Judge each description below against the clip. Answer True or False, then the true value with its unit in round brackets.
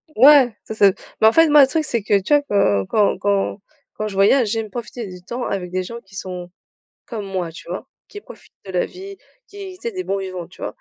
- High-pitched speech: True (210 Hz)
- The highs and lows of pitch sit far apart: True (6.1 semitones)